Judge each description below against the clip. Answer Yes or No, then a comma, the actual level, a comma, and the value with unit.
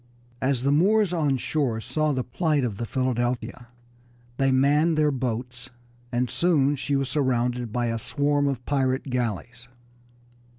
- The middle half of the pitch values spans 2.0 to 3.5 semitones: Yes, average, 3.0 semitones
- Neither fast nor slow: Yes, average, 145 wpm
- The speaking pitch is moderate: No, low, 130 Hz